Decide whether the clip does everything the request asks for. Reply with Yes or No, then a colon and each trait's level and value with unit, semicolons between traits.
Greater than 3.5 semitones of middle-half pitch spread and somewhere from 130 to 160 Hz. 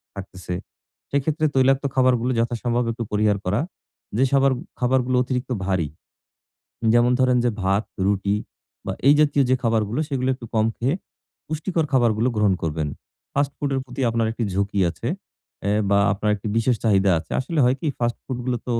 No: average, 4.1 semitones; low, 120 Hz